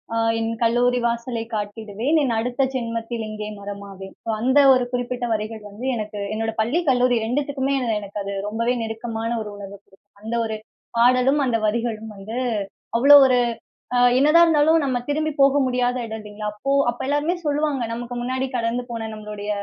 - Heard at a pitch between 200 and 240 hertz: Yes, high, 235 Hz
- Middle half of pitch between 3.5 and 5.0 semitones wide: No, average, 3.0 semitones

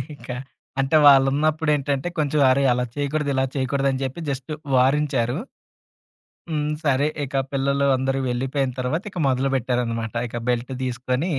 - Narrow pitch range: Yes, narrow, 2.1 semitones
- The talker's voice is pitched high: No, low, 135 Hz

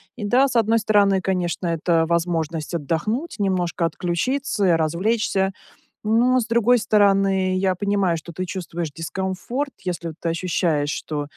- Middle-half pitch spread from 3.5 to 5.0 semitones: Yes, average, 4.1 semitones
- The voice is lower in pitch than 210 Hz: Yes, medium, 185 Hz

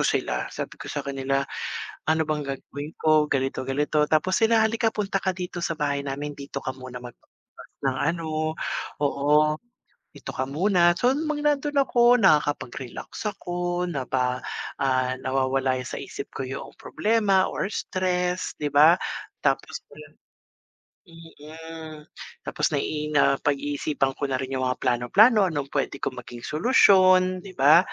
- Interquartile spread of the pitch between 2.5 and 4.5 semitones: No, average, 5.2 semitones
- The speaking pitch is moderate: Yes, medium, 150 Hz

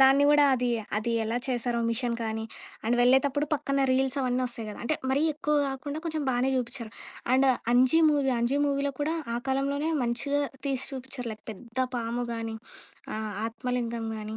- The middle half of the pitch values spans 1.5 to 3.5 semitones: Yes, average, 2.9 semitones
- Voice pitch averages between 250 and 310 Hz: Yes, very high, 255 Hz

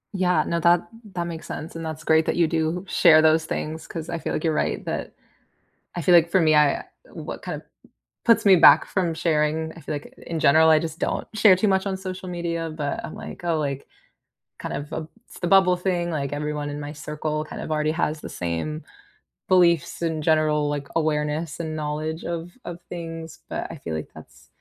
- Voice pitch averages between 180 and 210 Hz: No, medium, 160 Hz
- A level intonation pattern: Yes, narrow, 2.1 semitones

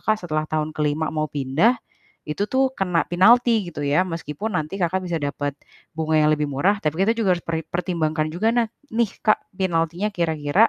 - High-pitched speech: No, medium, 170 Hz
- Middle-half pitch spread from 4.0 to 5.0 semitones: Yes, average, 4.5 semitones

